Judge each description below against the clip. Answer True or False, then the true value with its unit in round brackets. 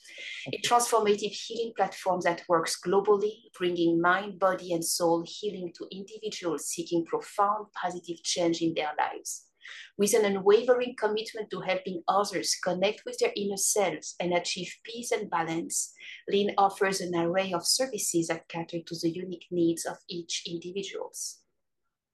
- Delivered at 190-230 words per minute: False (145 wpm)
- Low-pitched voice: False (190 Hz)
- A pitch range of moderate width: True (3.5 semitones)